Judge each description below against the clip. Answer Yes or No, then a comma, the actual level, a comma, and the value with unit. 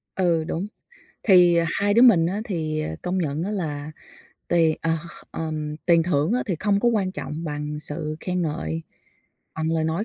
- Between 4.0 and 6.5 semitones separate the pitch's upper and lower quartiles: No, average, 3.3 semitones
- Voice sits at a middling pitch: Yes, medium, 165 Hz